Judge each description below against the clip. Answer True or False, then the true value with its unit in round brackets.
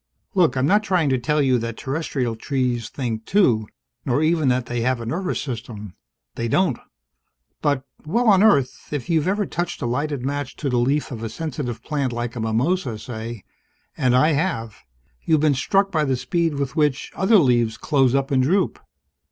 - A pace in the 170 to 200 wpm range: True (190 wpm)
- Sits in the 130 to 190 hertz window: True (135 Hz)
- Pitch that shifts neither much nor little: True (4.7 semitones)